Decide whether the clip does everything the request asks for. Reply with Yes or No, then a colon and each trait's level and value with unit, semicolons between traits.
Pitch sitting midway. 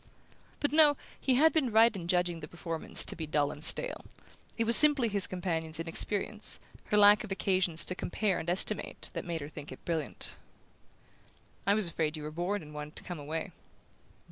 Yes: medium, 180 Hz